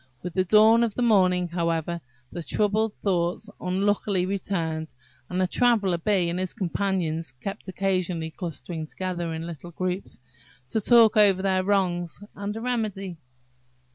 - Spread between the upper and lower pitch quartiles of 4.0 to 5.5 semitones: No, average, 3.0 semitones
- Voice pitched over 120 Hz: Yes, medium, 185 Hz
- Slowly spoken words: No, average, 145 wpm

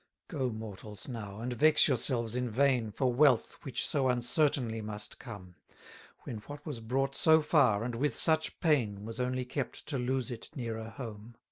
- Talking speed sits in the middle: Yes, average, 175 wpm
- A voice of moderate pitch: No, low, 125 Hz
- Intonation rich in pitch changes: No, average, 3.5 semitones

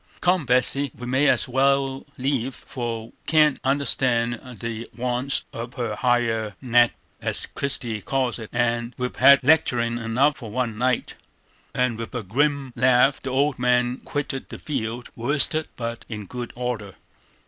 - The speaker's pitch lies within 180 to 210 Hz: No, low, 125 Hz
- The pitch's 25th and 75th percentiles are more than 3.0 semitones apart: No, narrow, 2.5 semitones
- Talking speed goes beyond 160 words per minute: No, average, 155 wpm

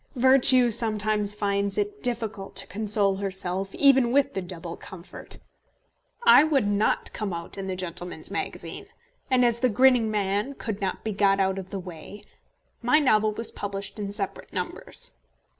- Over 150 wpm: Yes, average, 160 wpm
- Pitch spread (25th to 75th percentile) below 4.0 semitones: Yes, average, 3.6 semitones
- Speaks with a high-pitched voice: Yes, high, 205 Hz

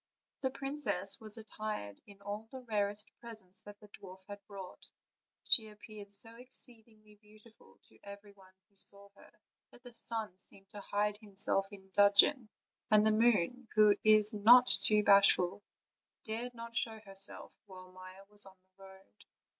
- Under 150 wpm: No, average, 155 wpm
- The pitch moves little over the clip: Yes, narrow, 2.2 semitones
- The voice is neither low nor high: No, high, 210 Hz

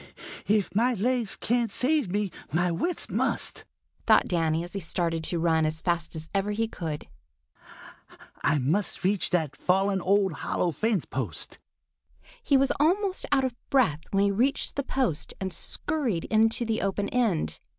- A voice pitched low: No, high, 195 Hz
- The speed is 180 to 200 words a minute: No, average, 160 wpm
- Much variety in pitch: Yes, wide, 6.0 semitones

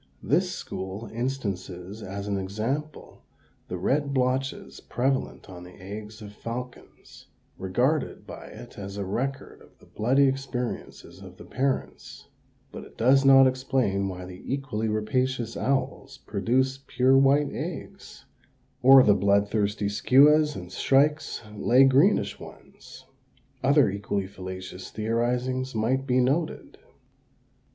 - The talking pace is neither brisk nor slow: No, slow, 130 wpm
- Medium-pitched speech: No, low, 125 Hz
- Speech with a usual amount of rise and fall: Yes, average, 4.9 semitones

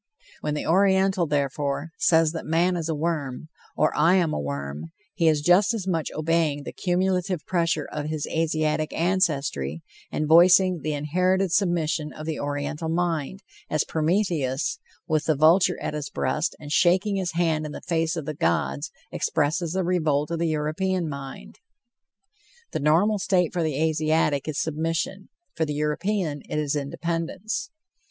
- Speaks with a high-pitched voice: No, medium, 160 Hz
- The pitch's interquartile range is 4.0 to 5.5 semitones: No, average, 2.9 semitones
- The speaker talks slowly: No, average, 160 wpm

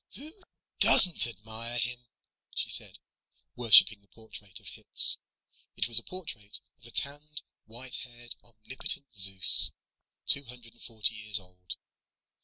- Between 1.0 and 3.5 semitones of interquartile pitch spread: Yes, average, 2.7 semitones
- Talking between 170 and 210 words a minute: No, slow, 135 wpm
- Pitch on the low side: Yes, low, 115 Hz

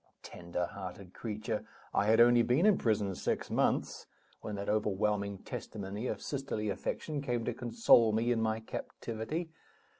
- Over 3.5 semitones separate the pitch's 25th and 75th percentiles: No, average, 3.0 semitones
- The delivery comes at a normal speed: Yes, average, 145 wpm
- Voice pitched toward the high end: No, low, 110 Hz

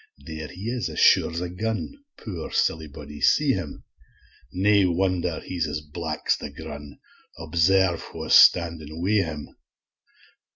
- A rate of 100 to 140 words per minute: Yes, slow, 135 wpm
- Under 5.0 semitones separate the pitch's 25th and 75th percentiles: Yes, average, 3.5 semitones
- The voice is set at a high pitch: No, very low, 85 Hz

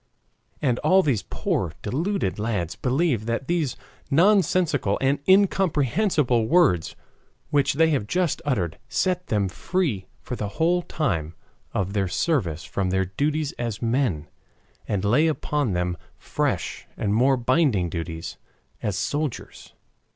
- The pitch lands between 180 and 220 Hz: No, low, 125 Hz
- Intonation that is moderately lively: No, wide, 8.2 semitones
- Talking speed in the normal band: No, slow, 130 wpm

